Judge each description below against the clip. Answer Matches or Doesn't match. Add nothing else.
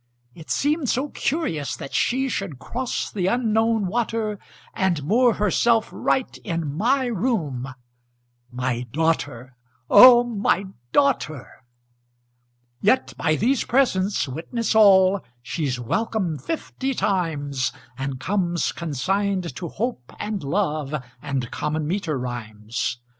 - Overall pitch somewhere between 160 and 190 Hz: Matches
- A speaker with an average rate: Doesn't match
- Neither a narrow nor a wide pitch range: Doesn't match